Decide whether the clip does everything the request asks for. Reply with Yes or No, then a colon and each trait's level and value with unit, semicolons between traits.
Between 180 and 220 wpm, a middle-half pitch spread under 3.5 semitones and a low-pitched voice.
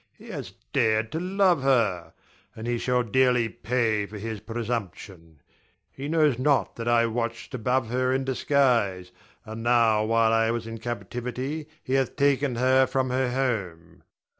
No: average, 160 wpm; average, 3.0 semitones; low, 120 Hz